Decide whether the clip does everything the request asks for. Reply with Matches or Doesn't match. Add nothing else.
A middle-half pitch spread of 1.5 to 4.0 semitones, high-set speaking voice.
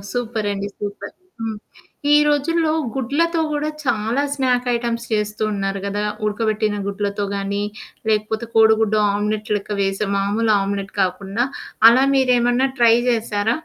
Matches